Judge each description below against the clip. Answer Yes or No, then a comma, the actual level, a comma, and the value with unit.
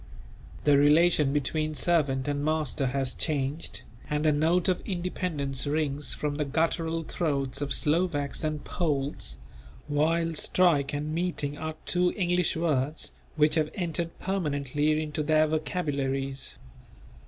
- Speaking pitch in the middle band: Yes, medium, 150 Hz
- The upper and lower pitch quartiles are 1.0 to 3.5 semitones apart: Yes, narrow, 2.5 semitones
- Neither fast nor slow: No, slow, 130 wpm